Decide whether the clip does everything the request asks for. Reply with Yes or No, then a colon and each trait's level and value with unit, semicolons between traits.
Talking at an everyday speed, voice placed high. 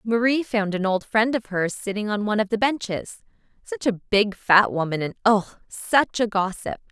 Yes: average, 190 wpm; high, 210 Hz